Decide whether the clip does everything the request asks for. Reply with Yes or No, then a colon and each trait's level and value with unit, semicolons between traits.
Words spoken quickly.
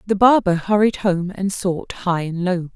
No: average, 195 wpm